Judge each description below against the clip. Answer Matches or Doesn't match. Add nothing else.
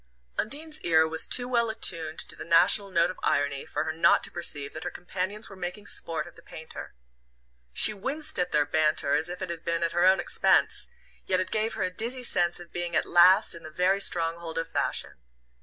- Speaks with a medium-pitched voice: Matches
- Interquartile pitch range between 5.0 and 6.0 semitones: Doesn't match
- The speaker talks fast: Matches